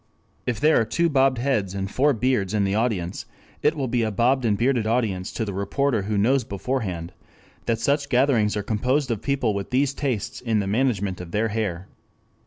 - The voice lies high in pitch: No, low, 115 Hz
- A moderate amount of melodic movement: Yes, average, 4.8 semitones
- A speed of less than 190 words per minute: No, average, 200 wpm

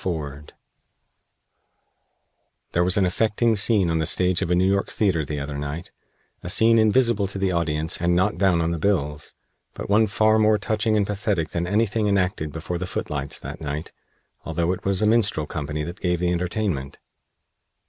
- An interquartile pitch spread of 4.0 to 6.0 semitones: Yes, average, 4.3 semitones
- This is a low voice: Yes, very low, 90 Hz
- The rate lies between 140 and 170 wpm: No, average, 180 wpm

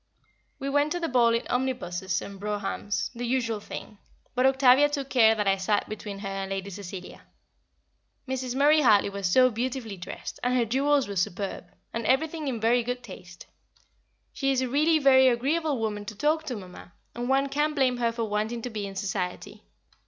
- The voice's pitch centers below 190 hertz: No, high, 240 Hz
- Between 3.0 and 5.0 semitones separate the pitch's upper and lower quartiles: Yes, average, 4.7 semitones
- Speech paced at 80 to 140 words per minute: No, average, 190 wpm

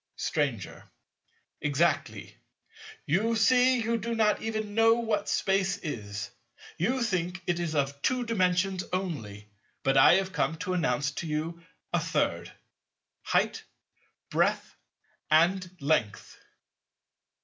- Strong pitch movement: Yes, wide, 6.6 semitones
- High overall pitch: No, medium, 180 Hz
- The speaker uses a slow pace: Yes, slow, 115 wpm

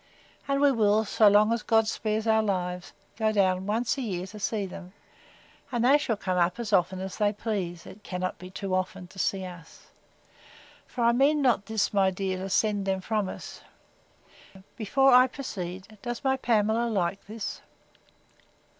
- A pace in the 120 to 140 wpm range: No, average, 175 wpm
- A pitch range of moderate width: Yes, average, 3.3 semitones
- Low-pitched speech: No, high, 205 Hz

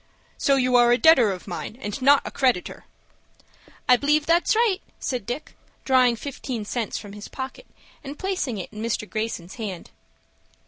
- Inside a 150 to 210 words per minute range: Yes, average, 165 wpm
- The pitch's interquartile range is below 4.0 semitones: No, average, 4.7 semitones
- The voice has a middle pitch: No, very high, 250 Hz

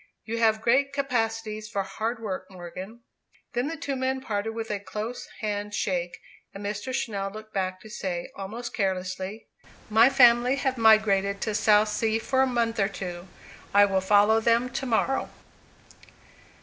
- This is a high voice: Yes, high, 220 Hz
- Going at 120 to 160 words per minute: Yes, average, 155 wpm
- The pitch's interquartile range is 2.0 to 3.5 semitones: Yes, average, 3.0 semitones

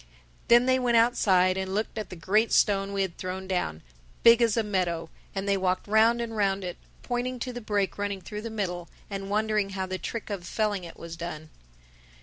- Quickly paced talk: Yes, fast, 210 wpm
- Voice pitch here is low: No, high, 200 Hz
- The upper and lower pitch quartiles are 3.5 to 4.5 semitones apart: No, average, 3.1 semitones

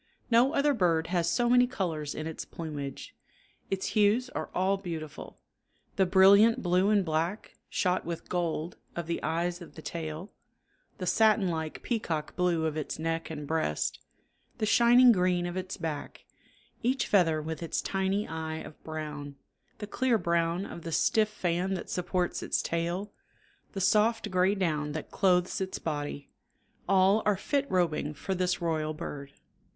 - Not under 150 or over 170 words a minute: Yes, average, 160 wpm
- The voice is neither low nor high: Yes, medium, 175 Hz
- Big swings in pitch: No, average, 3.8 semitones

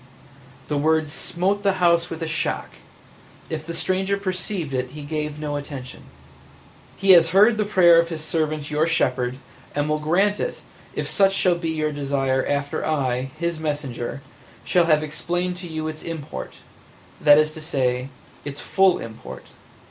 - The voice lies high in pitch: No, medium, 155 Hz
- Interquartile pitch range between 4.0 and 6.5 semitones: No, average, 3.2 semitones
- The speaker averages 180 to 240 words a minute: No, average, 170 wpm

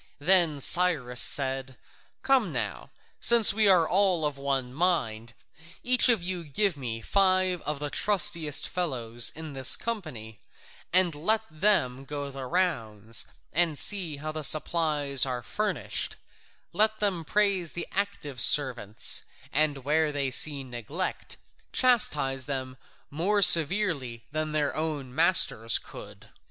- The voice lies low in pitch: No, medium, 155 Hz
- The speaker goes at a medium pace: No, slow, 130 wpm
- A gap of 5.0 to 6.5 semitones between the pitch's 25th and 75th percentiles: Yes, wide, 5.6 semitones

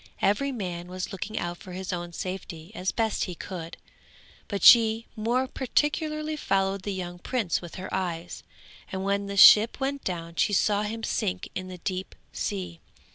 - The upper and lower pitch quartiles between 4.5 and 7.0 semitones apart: No, average, 3.6 semitones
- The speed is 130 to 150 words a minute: No, average, 175 wpm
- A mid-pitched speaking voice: No, high, 195 Hz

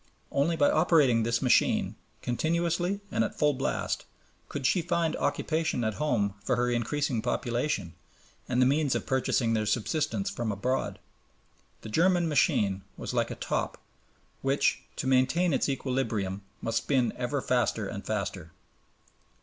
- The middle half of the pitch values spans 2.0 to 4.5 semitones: No, average, 5.0 semitones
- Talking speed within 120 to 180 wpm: Yes, average, 145 wpm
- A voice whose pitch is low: Yes, low, 125 Hz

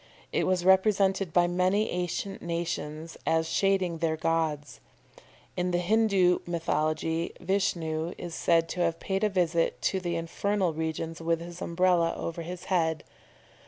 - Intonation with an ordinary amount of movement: No, narrow, 2.2 semitones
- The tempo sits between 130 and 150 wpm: Yes, average, 145 wpm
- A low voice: No, medium, 175 Hz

